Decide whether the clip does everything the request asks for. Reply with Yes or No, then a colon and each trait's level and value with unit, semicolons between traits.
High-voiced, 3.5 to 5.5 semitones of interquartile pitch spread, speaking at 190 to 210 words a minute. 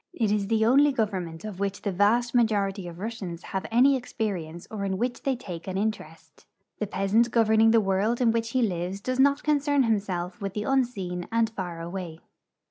Yes: high, 210 Hz; average, 3.8 semitones; fast, 205 wpm